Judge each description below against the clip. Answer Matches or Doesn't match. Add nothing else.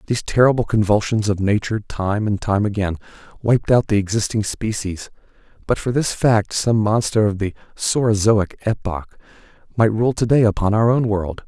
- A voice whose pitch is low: Matches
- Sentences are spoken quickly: Doesn't match